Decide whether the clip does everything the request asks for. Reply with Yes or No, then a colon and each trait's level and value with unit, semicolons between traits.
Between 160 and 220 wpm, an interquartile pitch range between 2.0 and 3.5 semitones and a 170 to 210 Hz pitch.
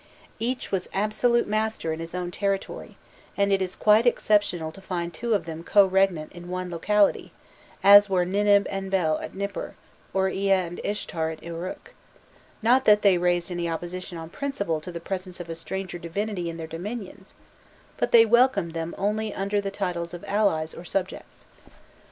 Yes: average, 180 wpm; average, 3.2 semitones; high, 190 Hz